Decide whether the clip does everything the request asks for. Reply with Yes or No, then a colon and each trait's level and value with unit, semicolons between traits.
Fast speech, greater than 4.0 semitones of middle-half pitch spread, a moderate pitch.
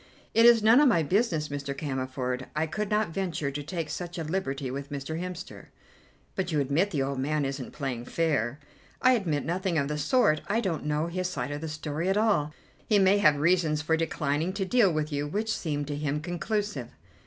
Yes: fast, 210 wpm; average, 4.7 semitones; medium, 155 Hz